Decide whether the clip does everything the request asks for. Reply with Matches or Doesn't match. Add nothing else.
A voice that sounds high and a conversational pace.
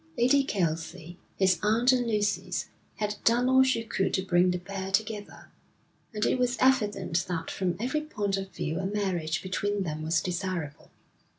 Matches